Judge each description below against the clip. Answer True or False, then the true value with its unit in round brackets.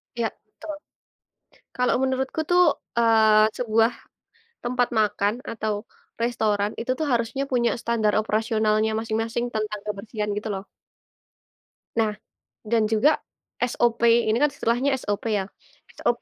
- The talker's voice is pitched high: True (225 Hz)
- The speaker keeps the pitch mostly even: True (2.0 semitones)